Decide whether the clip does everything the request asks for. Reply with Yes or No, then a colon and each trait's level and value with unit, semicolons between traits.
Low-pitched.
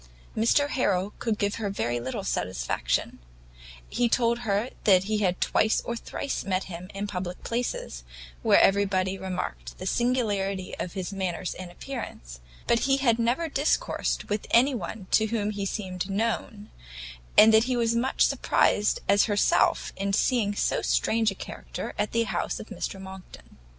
No: high, 205 Hz